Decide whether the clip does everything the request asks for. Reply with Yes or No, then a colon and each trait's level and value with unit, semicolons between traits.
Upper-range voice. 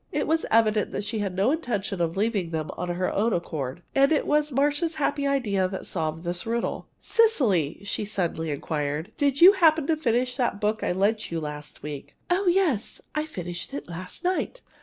Yes: high, 215 Hz